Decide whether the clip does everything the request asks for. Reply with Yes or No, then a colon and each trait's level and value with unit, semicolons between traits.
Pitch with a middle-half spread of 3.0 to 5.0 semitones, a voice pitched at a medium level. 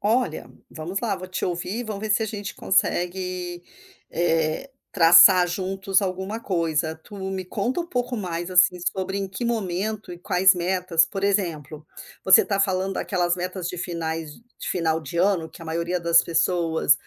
No: narrow, 2.6 semitones; medium, 180 Hz